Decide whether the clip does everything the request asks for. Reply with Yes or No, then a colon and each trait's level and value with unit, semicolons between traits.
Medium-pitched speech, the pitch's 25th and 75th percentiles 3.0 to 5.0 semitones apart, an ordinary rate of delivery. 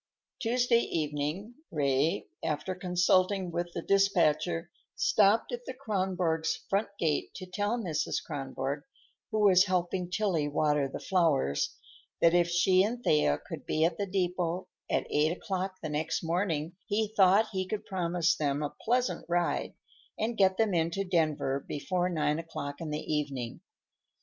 Yes: medium, 175 Hz; average, 4.2 semitones; average, 145 wpm